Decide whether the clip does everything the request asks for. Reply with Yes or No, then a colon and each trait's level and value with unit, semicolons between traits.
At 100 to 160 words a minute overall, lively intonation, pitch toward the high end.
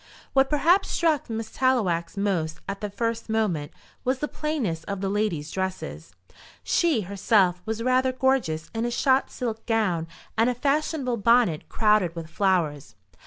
Yes: average, 155 wpm; wide, 5.9 semitones; high, 220 Hz